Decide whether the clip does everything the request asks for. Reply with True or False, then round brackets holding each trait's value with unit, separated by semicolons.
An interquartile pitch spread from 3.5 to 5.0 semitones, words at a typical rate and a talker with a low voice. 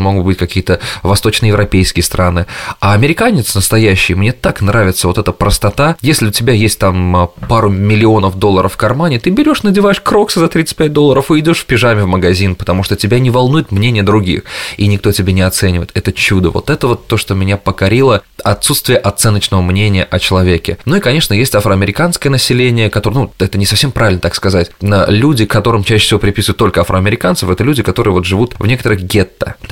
False (4.3 semitones; 185 wpm; 105 Hz)